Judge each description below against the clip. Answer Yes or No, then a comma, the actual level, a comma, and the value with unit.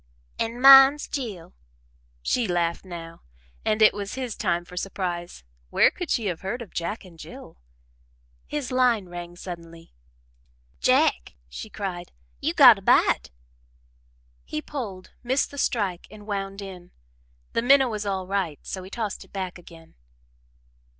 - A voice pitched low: No, high, 195 Hz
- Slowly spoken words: No, average, 150 wpm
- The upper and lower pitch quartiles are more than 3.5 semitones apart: Yes, average, 4.8 semitones